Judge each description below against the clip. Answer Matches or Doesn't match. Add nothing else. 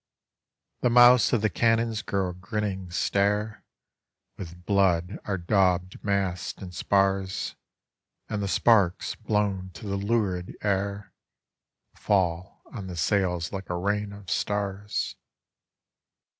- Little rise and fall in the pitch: Matches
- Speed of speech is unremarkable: Doesn't match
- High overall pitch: Doesn't match